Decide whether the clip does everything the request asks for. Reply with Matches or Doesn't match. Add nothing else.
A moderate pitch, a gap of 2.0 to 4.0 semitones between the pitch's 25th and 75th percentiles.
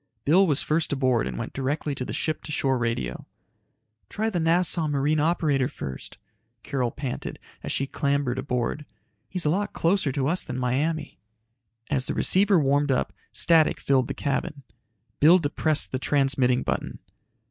Matches